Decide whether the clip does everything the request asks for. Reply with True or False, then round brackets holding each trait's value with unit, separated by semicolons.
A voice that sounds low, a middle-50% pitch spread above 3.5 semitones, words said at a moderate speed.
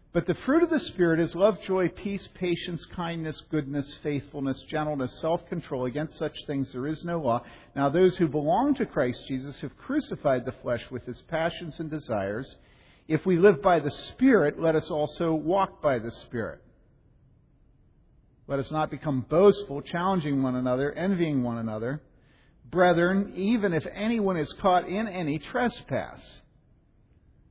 False (155 Hz; 4.8 semitones; 160 wpm)